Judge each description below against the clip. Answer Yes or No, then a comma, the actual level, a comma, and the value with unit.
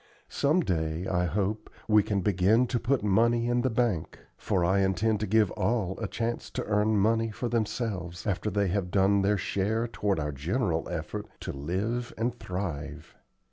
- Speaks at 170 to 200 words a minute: Yes, average, 180 wpm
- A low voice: Yes, low, 105 Hz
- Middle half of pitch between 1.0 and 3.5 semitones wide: No, average, 3.9 semitones